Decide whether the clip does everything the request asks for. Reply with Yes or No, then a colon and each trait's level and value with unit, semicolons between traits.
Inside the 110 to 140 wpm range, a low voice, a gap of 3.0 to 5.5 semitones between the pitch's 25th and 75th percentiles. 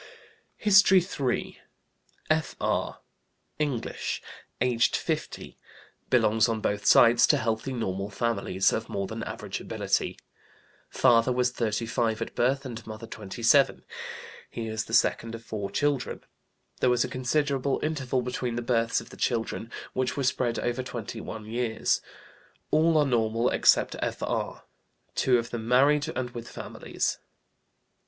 No: slow, 135 wpm; low, 120 Hz; narrow, 2.4 semitones